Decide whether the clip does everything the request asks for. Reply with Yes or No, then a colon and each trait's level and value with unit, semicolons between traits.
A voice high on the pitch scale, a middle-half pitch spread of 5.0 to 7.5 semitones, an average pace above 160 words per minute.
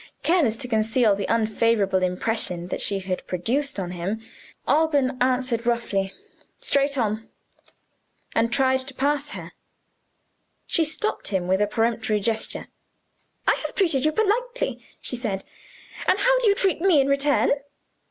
No: high, 235 Hz; wide, 5.6 semitones; average, 145 wpm